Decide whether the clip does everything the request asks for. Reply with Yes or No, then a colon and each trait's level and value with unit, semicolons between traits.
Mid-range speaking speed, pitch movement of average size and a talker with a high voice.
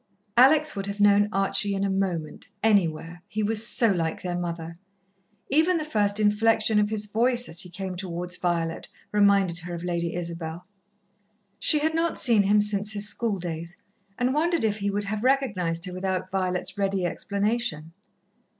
Yes: average, 170 wpm; average, 3.5 semitones; high, 200 Hz